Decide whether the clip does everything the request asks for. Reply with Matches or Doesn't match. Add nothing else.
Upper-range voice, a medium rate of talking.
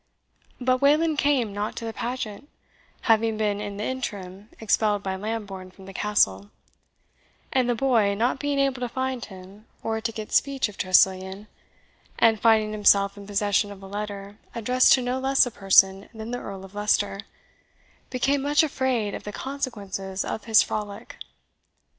Matches